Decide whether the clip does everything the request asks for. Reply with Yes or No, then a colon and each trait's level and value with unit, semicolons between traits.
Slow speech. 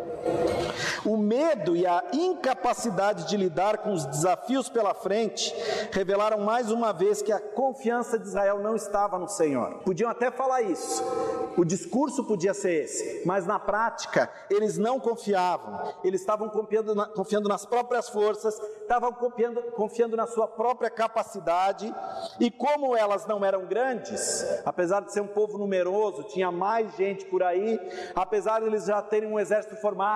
No: average, 160 wpm